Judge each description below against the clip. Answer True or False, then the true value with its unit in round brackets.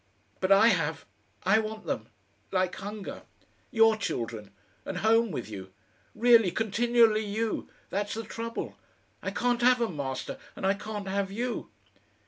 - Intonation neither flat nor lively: True (3.3 semitones)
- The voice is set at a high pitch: True (210 Hz)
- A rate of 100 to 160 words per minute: True (145 wpm)